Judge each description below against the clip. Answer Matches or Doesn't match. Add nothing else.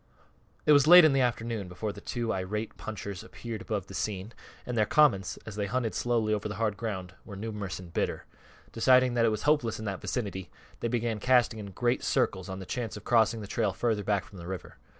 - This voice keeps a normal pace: Doesn't match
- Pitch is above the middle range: Doesn't match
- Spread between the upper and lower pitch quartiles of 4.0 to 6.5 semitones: Doesn't match